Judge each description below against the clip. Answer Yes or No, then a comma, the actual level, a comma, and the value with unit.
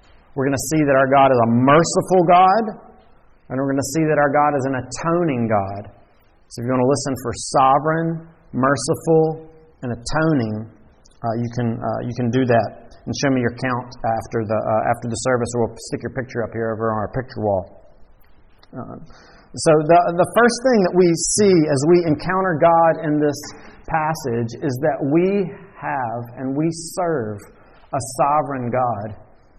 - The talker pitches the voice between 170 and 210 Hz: No, low, 135 Hz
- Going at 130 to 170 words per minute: No, average, 185 wpm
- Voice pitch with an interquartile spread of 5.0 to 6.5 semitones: Yes, wide, 5.5 semitones